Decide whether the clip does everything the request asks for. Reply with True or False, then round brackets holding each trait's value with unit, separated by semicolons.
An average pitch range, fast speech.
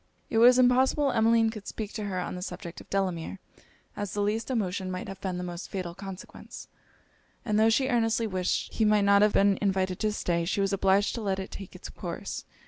True (3.0 semitones; 220 wpm)